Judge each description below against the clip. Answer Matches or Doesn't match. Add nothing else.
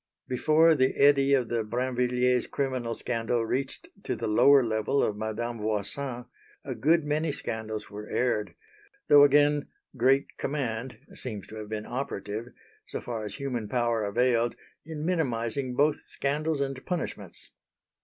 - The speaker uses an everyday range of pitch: Matches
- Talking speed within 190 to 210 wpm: Doesn't match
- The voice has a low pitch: Matches